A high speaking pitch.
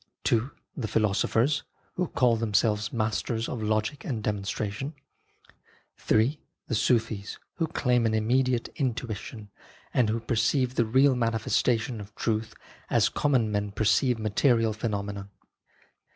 No: low, 115 Hz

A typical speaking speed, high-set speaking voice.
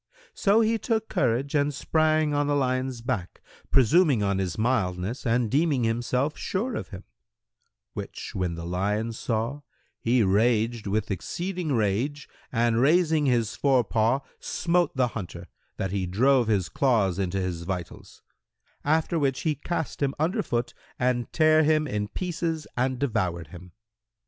No: average, 150 wpm; low, 125 Hz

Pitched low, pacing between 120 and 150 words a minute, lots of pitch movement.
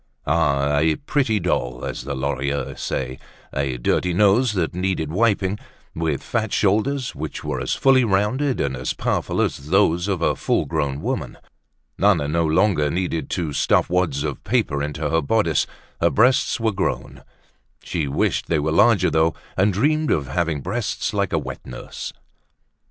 No: very low, 85 Hz; average, 165 wpm; wide, 6.2 semitones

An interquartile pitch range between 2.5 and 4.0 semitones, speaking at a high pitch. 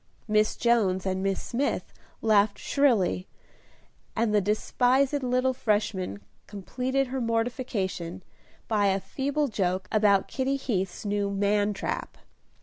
No: average, 4.4 semitones; high, 215 Hz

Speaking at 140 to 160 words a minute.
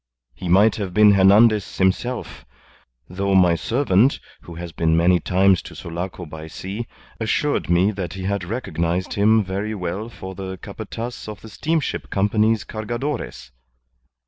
Yes: average, 145 wpm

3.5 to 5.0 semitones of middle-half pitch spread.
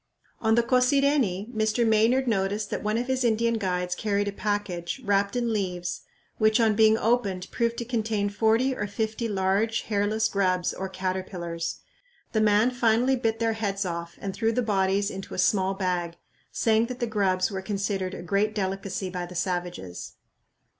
No: average, 3.0 semitones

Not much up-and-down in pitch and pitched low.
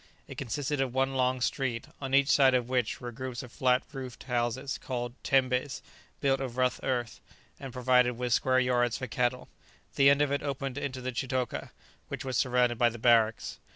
Yes: narrow, 1.6 semitones; low, 130 Hz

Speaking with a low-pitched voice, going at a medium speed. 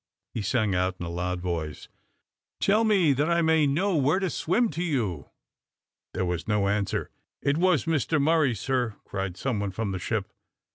Yes: low, 125 Hz; average, 185 wpm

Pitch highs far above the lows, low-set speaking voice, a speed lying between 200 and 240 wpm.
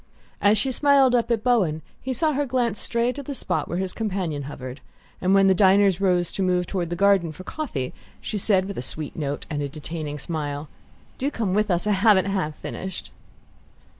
No: wide, 5.8 semitones; high, 190 Hz; fast, 205 wpm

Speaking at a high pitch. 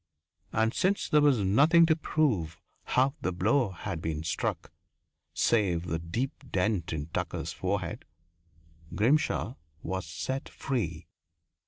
No: low, 105 Hz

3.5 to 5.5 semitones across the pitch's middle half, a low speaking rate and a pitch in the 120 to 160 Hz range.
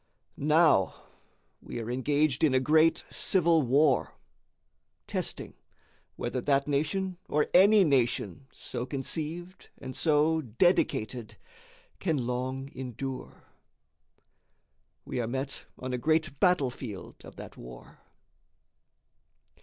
Yes: average, 4.0 semitones; slow, 105 wpm; medium, 140 Hz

